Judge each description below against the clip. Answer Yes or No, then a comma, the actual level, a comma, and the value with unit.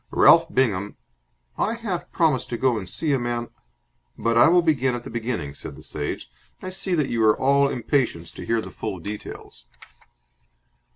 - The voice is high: No, low, 120 Hz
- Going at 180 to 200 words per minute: Yes, average, 185 wpm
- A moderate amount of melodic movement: No, wide, 5.8 semitones